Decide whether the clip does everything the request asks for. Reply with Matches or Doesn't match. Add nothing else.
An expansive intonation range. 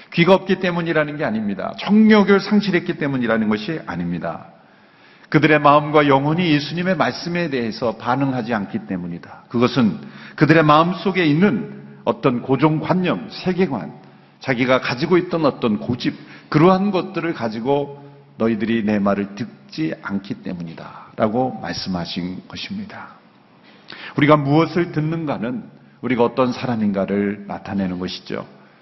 Matches